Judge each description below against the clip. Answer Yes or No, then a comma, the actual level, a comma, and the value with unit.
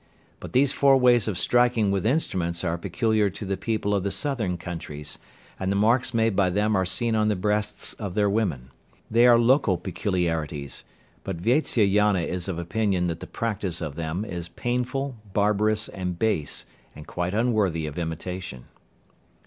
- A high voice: No, low, 100 Hz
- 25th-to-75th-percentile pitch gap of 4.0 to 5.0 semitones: Yes, average, 4.3 semitones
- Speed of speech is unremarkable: Yes, average, 170 wpm